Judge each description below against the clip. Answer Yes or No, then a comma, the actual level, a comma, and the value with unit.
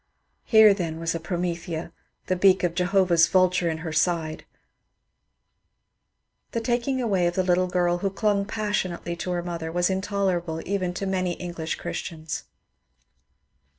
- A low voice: No, medium, 180 Hz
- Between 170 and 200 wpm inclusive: No, average, 155 wpm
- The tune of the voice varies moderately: No, narrow, 2.2 semitones